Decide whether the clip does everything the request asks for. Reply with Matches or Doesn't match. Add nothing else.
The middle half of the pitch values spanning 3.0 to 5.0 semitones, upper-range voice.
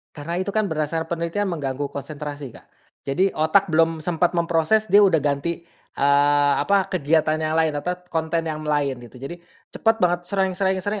Doesn't match